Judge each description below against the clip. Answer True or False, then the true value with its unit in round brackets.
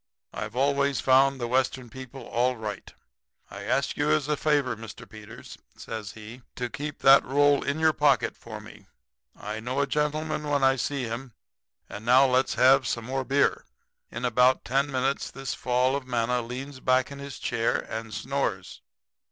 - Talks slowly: False (175 wpm)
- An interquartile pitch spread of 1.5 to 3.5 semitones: True (3.0 semitones)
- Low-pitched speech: True (130 Hz)